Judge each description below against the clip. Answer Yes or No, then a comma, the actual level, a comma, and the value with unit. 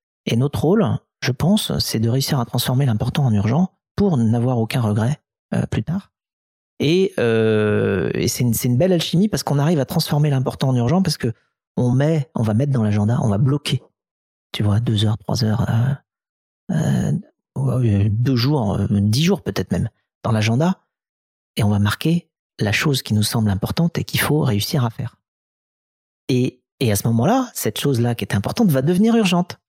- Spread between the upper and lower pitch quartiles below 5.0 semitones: No, wide, 5.4 semitones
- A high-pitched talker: No, low, 125 Hz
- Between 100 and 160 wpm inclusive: No, average, 190 wpm